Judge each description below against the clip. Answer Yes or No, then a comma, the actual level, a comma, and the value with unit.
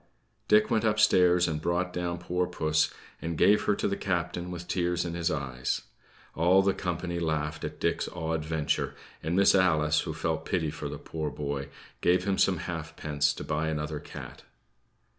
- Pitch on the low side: Yes, very low, 85 Hz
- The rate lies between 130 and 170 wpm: No, average, 180 wpm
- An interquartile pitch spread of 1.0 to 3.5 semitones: Yes, average, 2.7 semitones